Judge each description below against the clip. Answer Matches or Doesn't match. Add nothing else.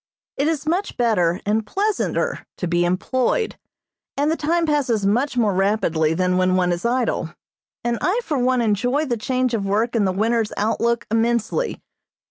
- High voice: Matches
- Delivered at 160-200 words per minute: Matches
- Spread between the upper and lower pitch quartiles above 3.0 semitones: Matches